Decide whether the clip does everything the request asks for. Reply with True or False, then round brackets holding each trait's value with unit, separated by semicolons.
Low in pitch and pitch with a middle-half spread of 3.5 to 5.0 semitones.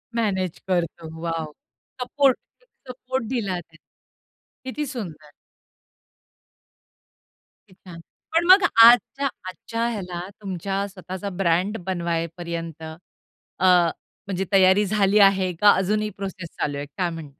False (190 Hz; 3.9 semitones)